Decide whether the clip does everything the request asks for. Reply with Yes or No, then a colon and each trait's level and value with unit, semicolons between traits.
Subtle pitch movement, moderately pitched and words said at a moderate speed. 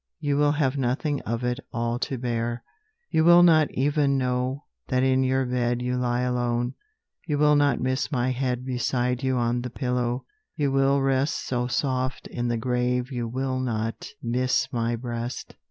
No: narrow, 1.8 semitones; low, 125 Hz; average, 175 wpm